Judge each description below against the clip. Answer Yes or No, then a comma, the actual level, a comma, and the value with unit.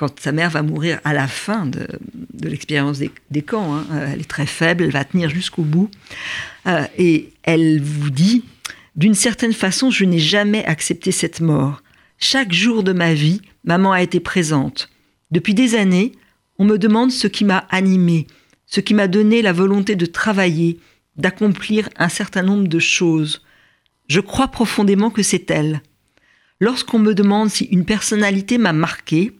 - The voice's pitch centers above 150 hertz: Yes, medium, 185 Hz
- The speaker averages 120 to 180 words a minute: Yes, average, 175 wpm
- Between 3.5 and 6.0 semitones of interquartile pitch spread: Yes, average, 5.0 semitones